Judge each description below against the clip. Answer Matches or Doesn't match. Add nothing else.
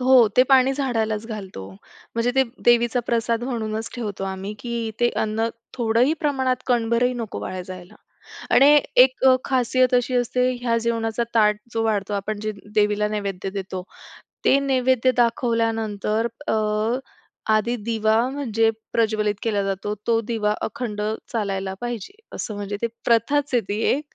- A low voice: Doesn't match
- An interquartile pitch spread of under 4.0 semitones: Matches